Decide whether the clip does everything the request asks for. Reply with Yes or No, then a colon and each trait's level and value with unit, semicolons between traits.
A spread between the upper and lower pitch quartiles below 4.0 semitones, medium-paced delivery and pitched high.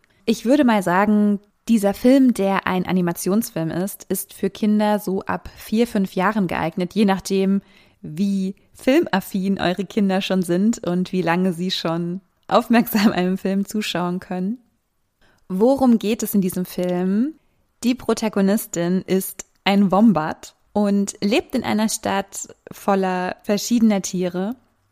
Yes: average, 2.9 semitones; average, 135 wpm; high, 195 Hz